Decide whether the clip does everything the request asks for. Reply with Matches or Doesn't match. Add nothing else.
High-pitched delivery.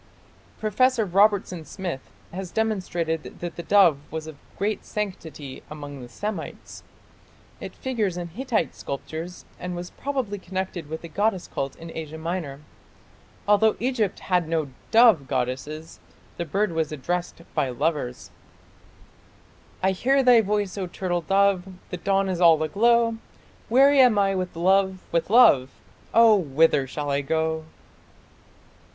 Doesn't match